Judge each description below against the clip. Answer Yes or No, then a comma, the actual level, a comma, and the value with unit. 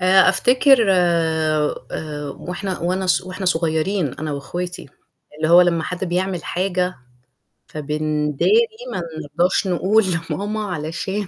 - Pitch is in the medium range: Yes, medium, 180 Hz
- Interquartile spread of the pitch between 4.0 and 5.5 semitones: No, average, 3.4 semitones